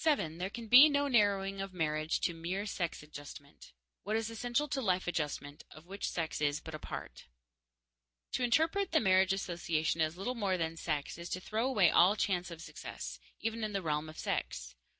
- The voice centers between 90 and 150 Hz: No, medium, 185 Hz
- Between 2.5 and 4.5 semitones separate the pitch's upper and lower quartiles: No, wide, 5.6 semitones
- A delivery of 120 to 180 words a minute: No, average, 190 wpm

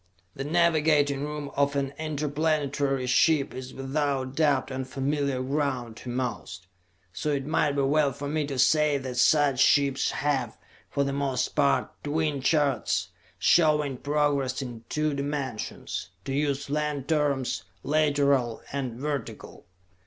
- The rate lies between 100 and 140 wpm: Yes, slow, 135 wpm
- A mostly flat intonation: Yes, narrow, 2.0 semitones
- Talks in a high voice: No, medium, 140 Hz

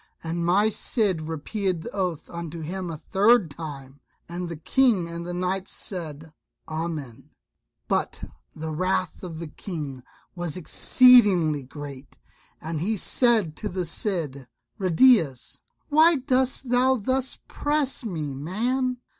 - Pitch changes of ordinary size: No, wide, 5.8 semitones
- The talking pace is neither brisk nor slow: No, slow, 130 wpm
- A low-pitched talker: No, medium, 175 Hz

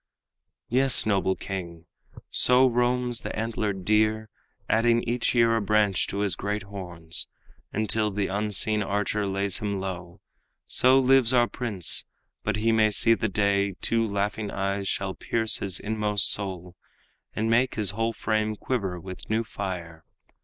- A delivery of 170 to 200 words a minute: No, average, 150 wpm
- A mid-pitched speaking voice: No, low, 105 Hz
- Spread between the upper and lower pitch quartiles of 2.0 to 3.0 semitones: Yes, narrow, 2.6 semitones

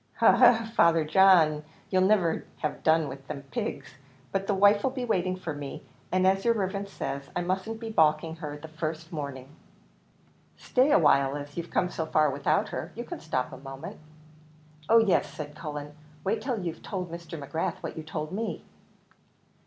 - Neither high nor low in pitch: Yes, medium, 165 Hz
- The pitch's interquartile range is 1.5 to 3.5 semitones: No, average, 4.7 semitones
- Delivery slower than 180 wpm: No, average, 185 wpm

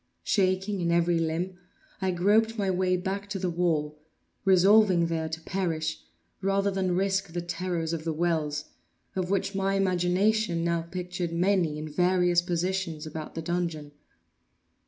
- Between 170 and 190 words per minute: No, average, 145 wpm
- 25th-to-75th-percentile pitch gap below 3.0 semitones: Yes, narrow, 2.5 semitones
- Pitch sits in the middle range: Yes, medium, 180 Hz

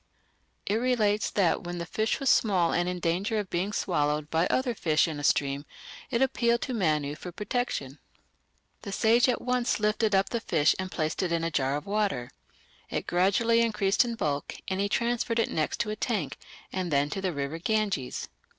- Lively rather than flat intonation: Yes, wide, 5.8 semitones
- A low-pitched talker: No, high, 195 Hz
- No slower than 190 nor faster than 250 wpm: Yes, average, 195 wpm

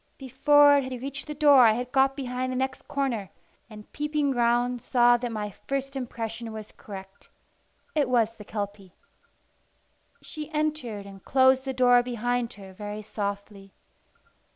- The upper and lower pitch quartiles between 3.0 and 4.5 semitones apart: Yes, average, 4.1 semitones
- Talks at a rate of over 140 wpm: Yes, average, 155 wpm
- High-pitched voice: Yes, high, 245 Hz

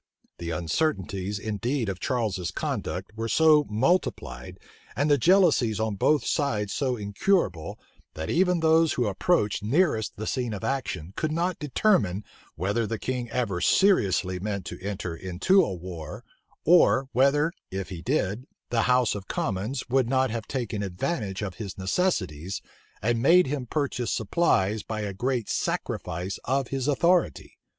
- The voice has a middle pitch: No, low, 115 Hz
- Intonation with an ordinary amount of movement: No, wide, 6.6 semitones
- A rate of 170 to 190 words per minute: No, average, 150 wpm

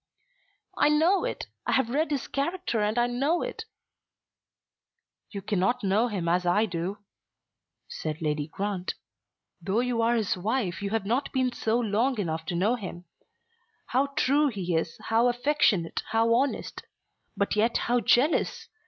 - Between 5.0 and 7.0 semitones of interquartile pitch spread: Yes, average, 5.3 semitones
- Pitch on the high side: Yes, high, 225 Hz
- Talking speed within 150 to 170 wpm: Yes, average, 155 wpm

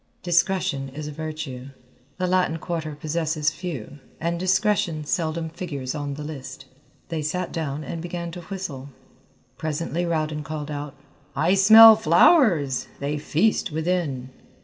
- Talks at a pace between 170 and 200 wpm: No, slow, 135 wpm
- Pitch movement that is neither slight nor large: Yes, average, 3.1 semitones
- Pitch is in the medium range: Yes, medium, 160 Hz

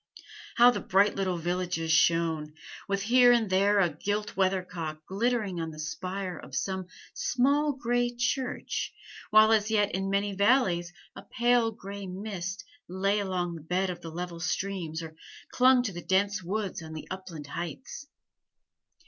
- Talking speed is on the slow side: No, average, 155 wpm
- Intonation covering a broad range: No, average, 3.7 semitones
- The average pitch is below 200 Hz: Yes, high, 190 Hz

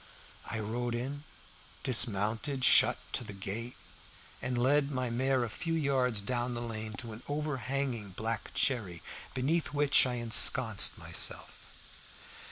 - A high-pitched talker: No, low, 120 Hz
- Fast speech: No, average, 140 wpm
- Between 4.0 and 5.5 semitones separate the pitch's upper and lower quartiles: No, average, 3.3 semitones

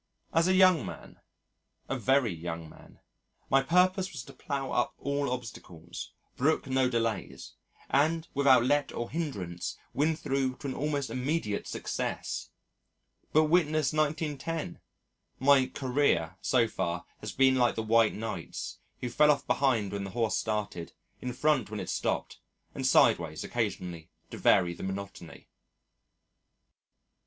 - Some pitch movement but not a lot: No, wide, 5.9 semitones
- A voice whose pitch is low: Yes, low, 130 Hz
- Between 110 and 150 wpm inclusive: Yes, average, 140 wpm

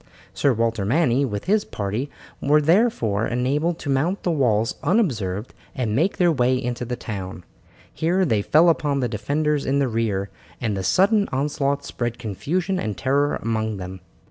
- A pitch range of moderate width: No, wide, 6.0 semitones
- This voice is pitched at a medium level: No, low, 130 Hz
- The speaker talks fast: No, average, 170 wpm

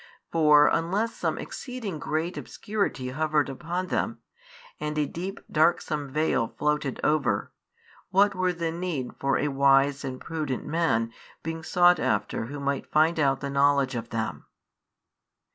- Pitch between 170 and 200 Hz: No, medium, 150 Hz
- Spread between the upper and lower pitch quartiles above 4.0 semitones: No, average, 3.6 semitones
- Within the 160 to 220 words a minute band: No, average, 145 wpm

